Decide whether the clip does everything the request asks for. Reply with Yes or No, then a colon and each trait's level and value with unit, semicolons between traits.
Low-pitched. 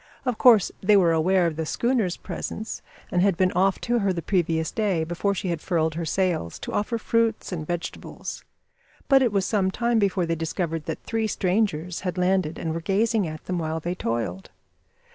No: medium, 185 Hz